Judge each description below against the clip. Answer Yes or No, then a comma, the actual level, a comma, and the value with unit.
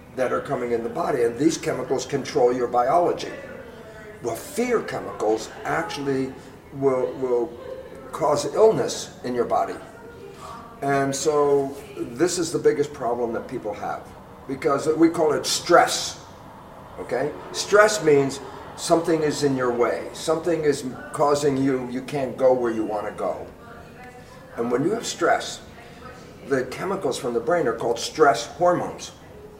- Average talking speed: No, fast, 145 wpm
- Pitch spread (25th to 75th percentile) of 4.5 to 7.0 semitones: Yes, average, 5.0 semitones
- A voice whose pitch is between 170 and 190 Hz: No, medium, 140 Hz